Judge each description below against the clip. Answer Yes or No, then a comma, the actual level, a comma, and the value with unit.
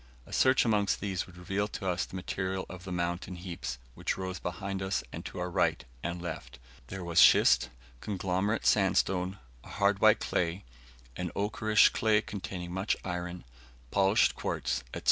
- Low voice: Yes, very low, 95 Hz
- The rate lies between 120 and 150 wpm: No, average, 165 wpm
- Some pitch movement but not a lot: No, narrow, 2.2 semitones